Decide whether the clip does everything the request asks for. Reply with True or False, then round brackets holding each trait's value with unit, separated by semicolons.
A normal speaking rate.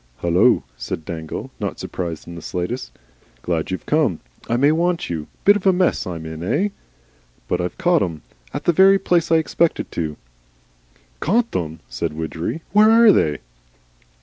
True (170 wpm)